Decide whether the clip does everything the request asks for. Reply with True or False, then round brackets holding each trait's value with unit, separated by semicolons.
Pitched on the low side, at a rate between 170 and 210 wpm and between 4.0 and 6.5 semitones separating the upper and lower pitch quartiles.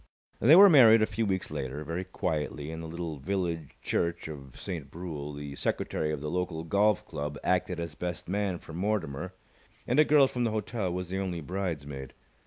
True (85 Hz; 195 wpm; 4.5 semitones)